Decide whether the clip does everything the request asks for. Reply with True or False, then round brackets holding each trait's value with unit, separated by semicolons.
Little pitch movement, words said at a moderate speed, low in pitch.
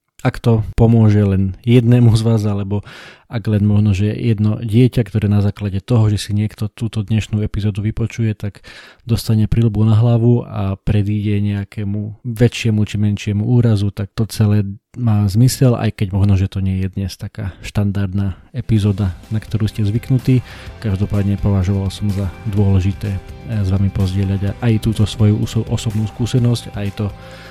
True (2.2 semitones; 155 wpm; 105 Hz)